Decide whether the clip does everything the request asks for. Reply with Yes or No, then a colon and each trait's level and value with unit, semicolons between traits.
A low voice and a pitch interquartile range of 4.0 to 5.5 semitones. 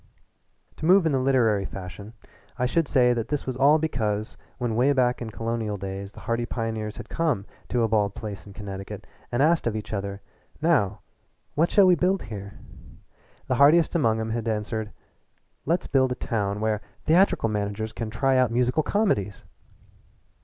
Yes: low, 115 Hz; average, 4.6 semitones